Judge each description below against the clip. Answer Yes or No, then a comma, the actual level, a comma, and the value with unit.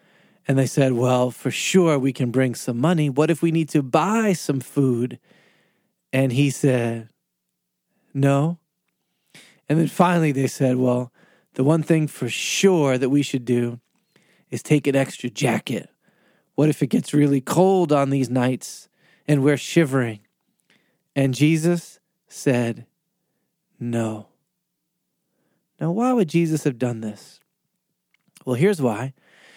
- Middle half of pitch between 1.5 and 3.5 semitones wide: No, average, 4.8 semitones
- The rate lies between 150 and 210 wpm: No, average, 140 wpm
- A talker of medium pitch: Yes, medium, 145 Hz